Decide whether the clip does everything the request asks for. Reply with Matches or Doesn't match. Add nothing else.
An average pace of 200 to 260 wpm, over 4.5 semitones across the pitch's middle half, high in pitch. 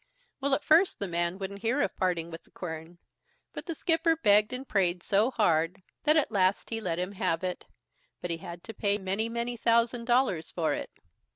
Matches